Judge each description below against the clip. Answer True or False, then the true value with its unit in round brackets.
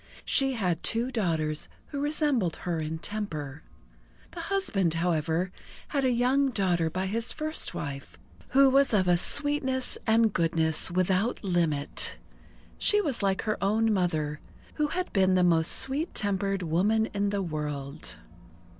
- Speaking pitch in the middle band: False (195 Hz)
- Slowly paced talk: False (145 wpm)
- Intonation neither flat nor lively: False (7.3 semitones)